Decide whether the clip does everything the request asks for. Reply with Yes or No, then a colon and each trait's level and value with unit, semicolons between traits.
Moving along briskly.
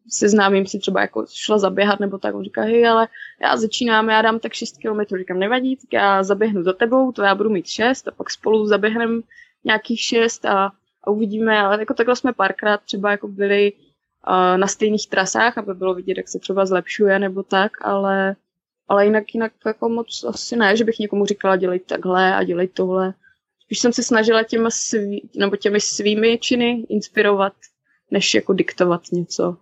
Yes: fast, 190 wpm